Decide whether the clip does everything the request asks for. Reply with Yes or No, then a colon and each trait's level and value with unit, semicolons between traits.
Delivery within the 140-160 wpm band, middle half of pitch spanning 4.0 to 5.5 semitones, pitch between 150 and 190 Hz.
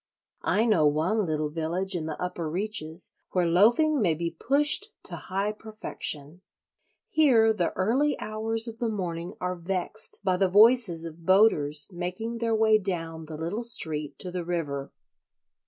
Yes: average, 155 wpm; average, 5.1 semitones; medium, 185 Hz